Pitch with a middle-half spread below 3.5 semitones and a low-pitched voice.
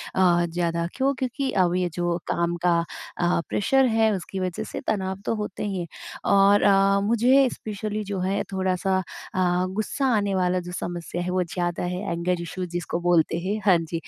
No: average, 2.8 semitones; medium, 185 Hz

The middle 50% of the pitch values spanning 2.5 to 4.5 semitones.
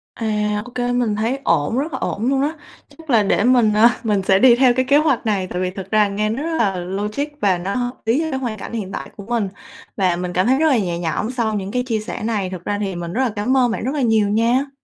Yes: average, 4.1 semitones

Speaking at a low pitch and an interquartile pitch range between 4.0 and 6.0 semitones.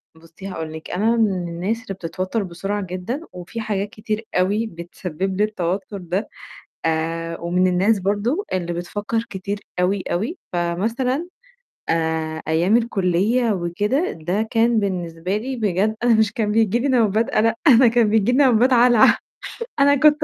No: high, 205 Hz; average, 4.4 semitones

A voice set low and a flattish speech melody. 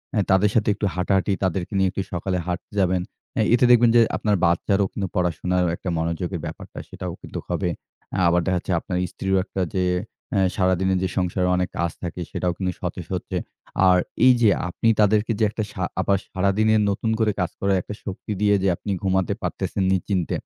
Yes: very low, 95 Hz; narrow, 2.1 semitones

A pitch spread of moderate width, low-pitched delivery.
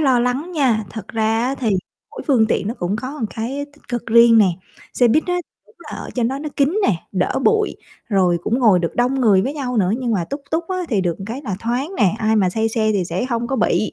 No: average, 4.0 semitones; high, 235 Hz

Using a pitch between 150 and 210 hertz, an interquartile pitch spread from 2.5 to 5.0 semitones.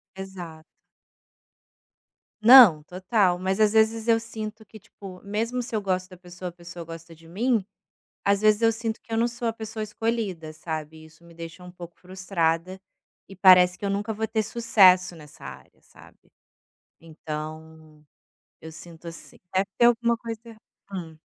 Yes: high, 190 Hz; average, 4.7 semitones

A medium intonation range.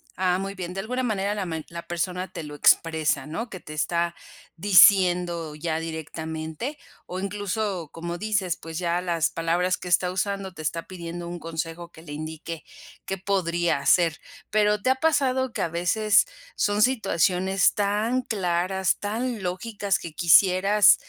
Yes: average, 3.4 semitones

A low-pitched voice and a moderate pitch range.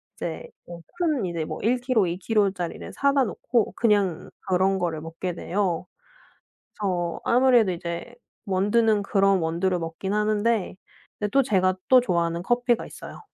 No: high, 195 Hz; average, 4.8 semitones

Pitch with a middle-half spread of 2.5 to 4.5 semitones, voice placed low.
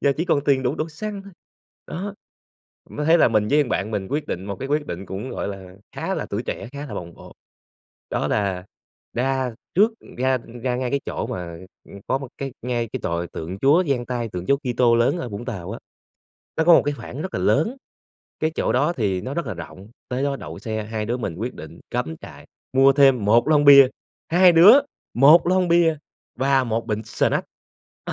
No: wide, 5.6 semitones; low, 130 Hz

